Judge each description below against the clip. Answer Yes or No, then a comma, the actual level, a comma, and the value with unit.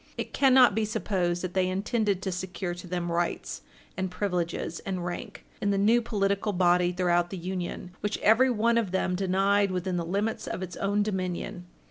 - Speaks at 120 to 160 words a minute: No, average, 185 wpm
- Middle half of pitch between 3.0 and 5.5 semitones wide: No, narrow, 2.5 semitones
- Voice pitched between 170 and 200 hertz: Yes, high, 190 Hz